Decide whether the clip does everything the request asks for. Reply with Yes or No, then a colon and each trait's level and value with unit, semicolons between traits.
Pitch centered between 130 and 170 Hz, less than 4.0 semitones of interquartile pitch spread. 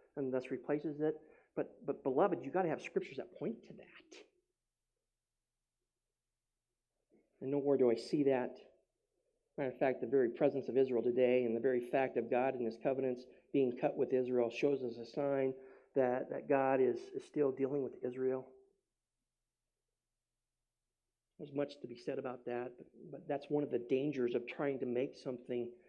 Yes: low, 135 Hz; average, 2.7 semitones